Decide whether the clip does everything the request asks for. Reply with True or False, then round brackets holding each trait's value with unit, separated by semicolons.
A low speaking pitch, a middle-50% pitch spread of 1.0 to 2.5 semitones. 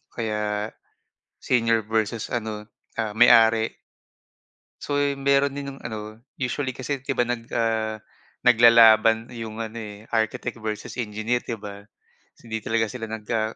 True (115 Hz; 1.8 semitones)